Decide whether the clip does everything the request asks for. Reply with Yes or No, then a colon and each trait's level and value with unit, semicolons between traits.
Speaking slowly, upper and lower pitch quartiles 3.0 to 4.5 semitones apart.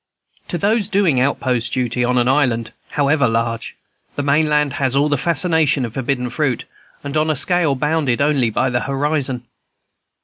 No: average, 170 wpm; average, 3.4 semitones